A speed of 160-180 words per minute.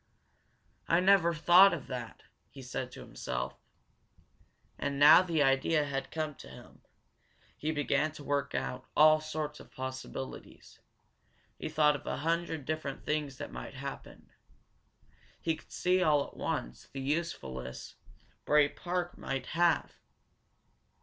No: average, 140 wpm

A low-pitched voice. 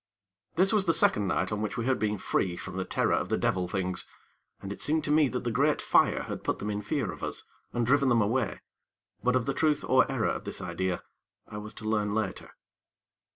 Yes: low, 110 Hz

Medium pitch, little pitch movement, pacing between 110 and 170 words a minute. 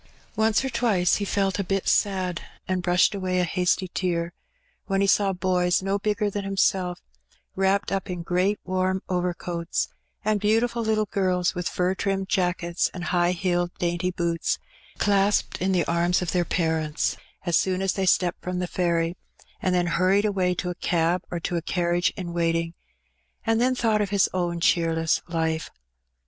No: medium, 180 Hz; narrow, 2.1 semitones; average, 180 wpm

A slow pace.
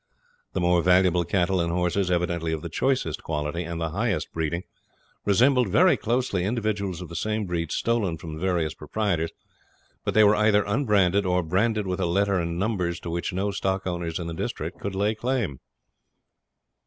No: average, 180 wpm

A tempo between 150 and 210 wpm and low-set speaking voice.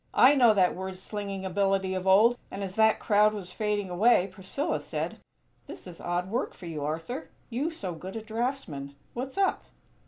No: average, 185 wpm; high, 200 Hz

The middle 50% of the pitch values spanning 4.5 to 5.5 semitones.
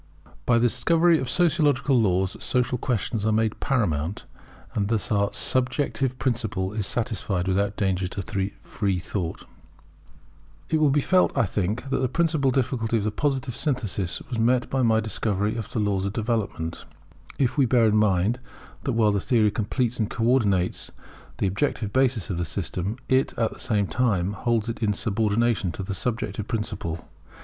No: average, 4.1 semitones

